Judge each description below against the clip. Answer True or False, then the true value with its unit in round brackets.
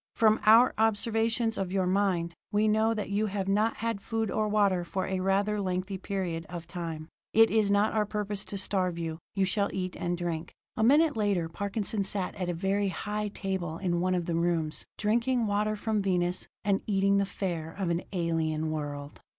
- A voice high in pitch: True (195 Hz)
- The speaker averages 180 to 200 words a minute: True (195 wpm)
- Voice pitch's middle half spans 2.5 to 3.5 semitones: True (3.2 semitones)